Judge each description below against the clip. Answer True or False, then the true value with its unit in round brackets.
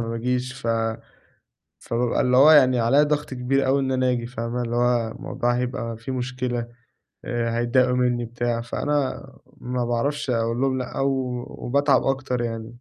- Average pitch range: False (1.8 semitones)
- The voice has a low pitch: True (125 Hz)